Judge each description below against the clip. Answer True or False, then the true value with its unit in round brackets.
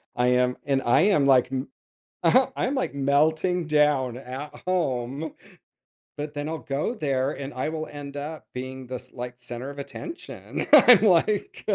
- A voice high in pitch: False (140 Hz)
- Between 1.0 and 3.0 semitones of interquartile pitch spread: False (3.5 semitones)